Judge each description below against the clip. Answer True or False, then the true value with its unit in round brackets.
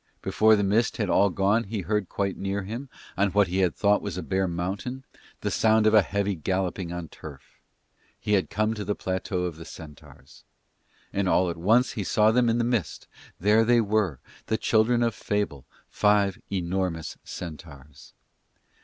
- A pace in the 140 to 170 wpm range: False (180 wpm)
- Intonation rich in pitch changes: False (3.3 semitones)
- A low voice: True (100 Hz)